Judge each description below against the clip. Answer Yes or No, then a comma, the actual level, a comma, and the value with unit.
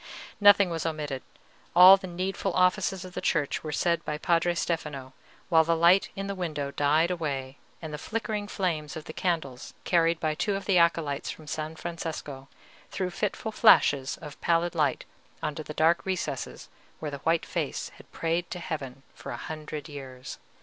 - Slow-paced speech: No, average, 175 wpm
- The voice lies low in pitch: No, medium, 165 Hz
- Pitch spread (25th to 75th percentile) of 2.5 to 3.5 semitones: Yes, average, 3.1 semitones